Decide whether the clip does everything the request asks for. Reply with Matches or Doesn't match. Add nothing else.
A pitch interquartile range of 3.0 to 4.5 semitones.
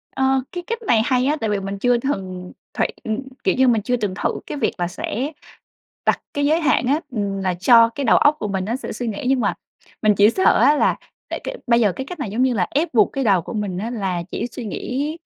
Doesn't match